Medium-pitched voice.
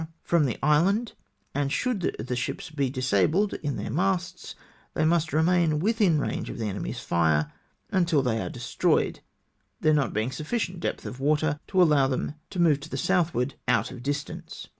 Yes: medium, 150 Hz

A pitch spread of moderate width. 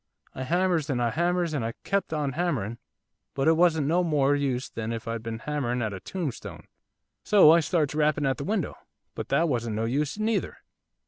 No: wide, 5.8 semitones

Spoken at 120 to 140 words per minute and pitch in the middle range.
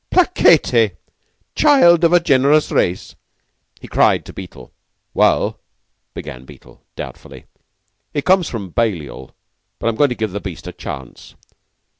No: slow, 135 wpm; low, 115 Hz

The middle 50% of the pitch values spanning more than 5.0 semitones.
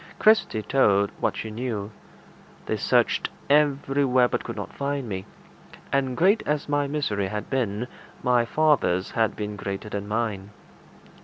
Yes: wide, 5.4 semitones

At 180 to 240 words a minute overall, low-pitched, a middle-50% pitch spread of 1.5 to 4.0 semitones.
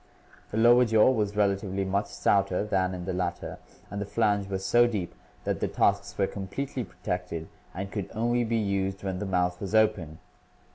Yes: average, 185 wpm; low, 100 Hz; narrow, 2.6 semitones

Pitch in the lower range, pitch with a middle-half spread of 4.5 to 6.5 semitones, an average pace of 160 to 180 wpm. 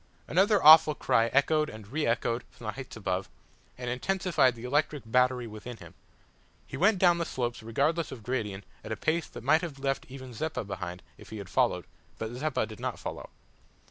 No: low, 130 Hz; wide, 5.5 semitones; average, 195 wpm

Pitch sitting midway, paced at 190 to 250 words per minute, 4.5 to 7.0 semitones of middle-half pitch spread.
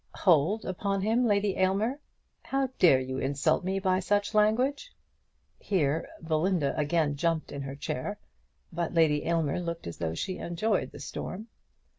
No: medium, 175 Hz; average, 150 wpm; average, 5.3 semitones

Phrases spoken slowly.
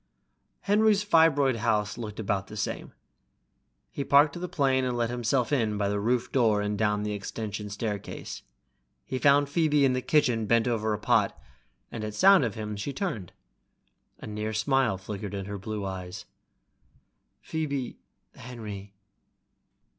No: average, 155 wpm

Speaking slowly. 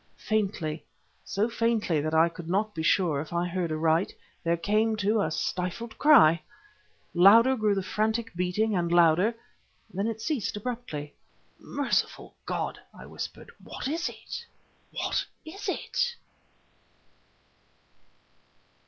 Yes: slow, 130 wpm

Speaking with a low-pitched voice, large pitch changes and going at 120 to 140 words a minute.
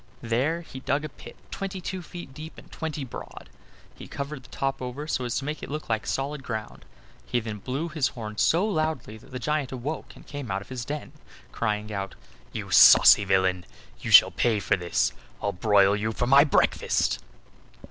No: low, 130 Hz; wide, 5.9 semitones; average, 200 wpm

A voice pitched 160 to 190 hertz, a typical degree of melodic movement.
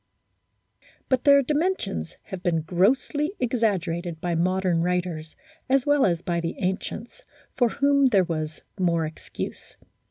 No: medium, 185 Hz; wide, 7.5 semitones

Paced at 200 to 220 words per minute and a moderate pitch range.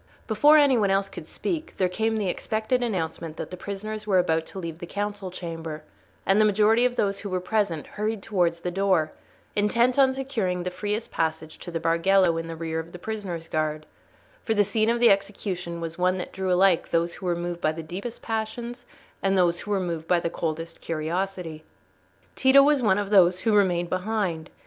Yes: fast, 205 wpm; average, 4.2 semitones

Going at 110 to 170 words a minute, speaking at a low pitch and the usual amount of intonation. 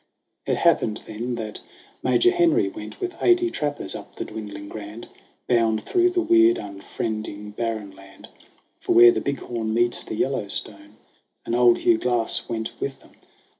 Yes: average, 160 wpm; low, 115 Hz; average, 4.6 semitones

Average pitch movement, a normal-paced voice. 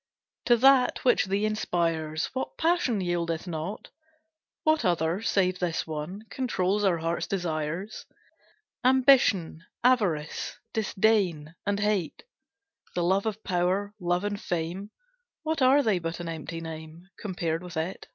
No: average, 4.4 semitones; slow, 130 wpm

